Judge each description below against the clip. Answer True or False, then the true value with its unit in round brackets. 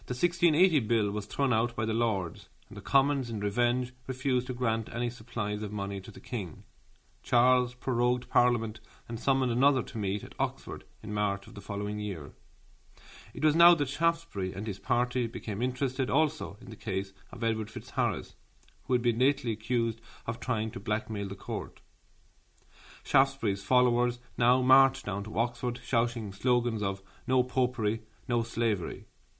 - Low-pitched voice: True (115 Hz)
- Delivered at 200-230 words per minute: False (170 wpm)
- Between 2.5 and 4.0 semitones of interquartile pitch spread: True (3.6 semitones)